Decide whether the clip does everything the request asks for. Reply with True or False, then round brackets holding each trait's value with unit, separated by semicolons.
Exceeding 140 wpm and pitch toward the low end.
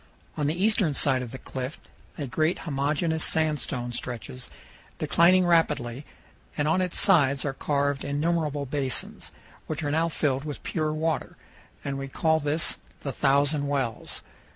False (150 wpm; 145 Hz)